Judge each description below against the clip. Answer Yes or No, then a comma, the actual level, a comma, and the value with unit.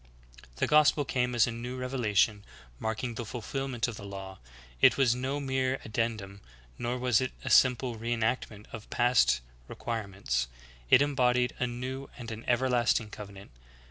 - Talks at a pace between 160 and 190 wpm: Yes, average, 170 wpm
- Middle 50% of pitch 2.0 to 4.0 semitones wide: Yes, average, 2.9 semitones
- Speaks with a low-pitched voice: Yes, low, 120 Hz